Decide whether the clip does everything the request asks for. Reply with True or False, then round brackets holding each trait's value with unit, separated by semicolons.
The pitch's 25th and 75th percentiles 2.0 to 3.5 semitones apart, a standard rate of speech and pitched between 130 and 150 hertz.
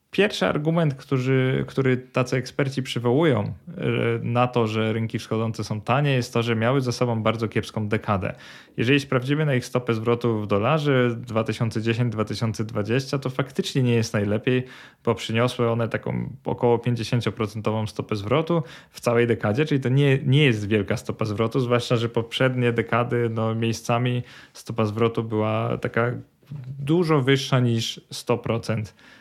False (2.8 semitones; 145 wpm; 120 Hz)